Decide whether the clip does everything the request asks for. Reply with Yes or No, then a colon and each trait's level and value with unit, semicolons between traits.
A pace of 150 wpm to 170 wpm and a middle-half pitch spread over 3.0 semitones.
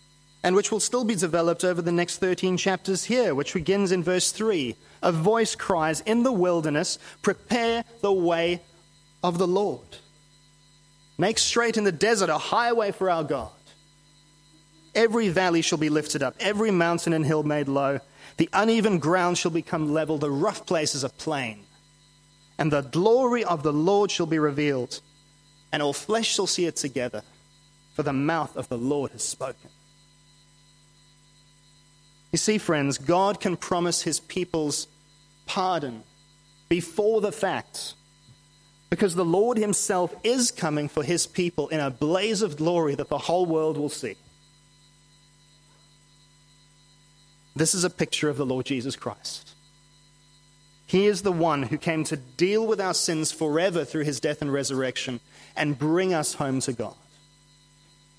Yes: average, 155 wpm; average, 4.1 semitones